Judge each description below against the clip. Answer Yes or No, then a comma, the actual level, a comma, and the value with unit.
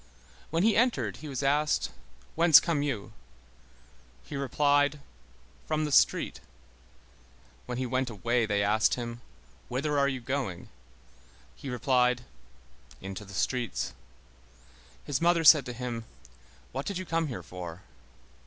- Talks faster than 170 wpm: No, slow, 135 wpm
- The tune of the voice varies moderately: Yes, average, 4.1 semitones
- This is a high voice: No, low, 130 Hz